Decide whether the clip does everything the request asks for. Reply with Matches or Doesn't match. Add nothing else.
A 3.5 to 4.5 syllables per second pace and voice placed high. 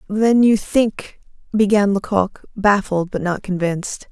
Matches